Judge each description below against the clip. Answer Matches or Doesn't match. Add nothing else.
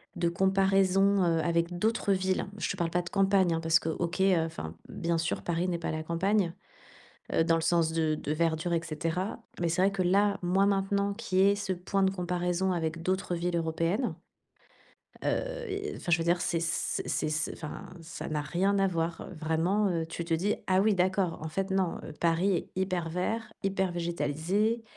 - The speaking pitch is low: Doesn't match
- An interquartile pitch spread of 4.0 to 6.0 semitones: Doesn't match